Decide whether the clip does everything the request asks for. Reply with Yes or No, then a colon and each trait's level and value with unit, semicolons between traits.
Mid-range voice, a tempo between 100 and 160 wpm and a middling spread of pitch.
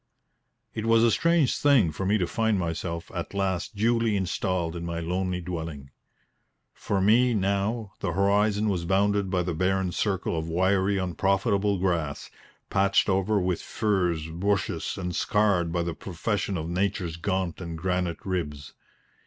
No: very low, 95 Hz; average, 155 wpm; average, 3.0 semitones